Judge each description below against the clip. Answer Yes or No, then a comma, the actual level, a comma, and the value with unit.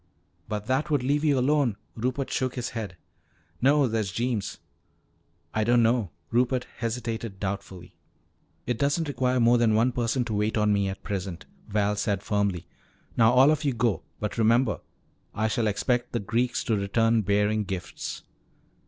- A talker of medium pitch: No, low, 115 Hz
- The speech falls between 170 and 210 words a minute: No, average, 160 wpm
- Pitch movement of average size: Yes, average, 3.4 semitones